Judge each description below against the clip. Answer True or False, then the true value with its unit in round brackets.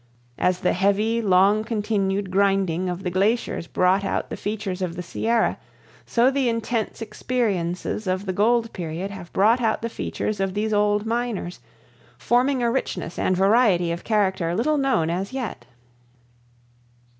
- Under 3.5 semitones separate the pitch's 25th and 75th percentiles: False (3.8 semitones)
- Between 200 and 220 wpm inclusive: False (155 wpm)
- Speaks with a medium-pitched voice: False (205 Hz)